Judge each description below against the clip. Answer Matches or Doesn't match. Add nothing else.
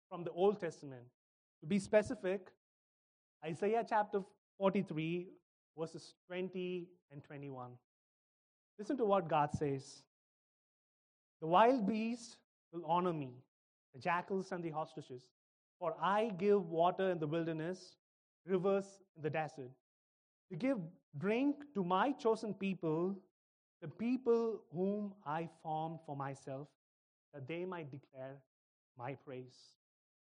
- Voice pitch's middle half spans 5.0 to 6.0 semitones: Matches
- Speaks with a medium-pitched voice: Matches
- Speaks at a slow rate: Matches